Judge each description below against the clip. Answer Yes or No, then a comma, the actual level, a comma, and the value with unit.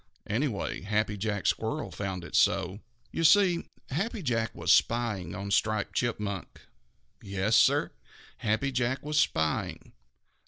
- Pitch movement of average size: Yes, average, 4.8 semitones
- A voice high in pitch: No, low, 110 Hz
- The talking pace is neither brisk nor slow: No, slow, 125 wpm